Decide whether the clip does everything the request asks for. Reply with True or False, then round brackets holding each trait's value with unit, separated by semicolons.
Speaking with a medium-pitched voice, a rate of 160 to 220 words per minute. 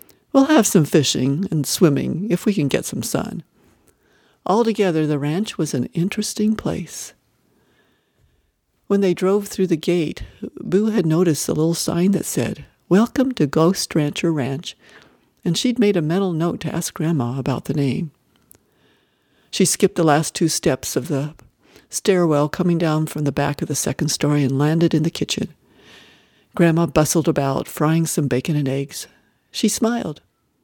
True (165 Hz; 165 wpm)